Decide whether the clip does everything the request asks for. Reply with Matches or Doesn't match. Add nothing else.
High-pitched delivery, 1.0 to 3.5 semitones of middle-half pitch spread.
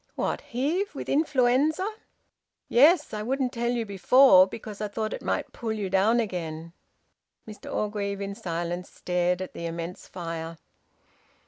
Doesn't match